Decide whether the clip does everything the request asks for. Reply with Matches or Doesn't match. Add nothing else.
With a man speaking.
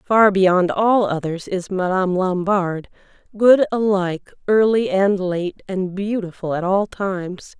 Doesn't match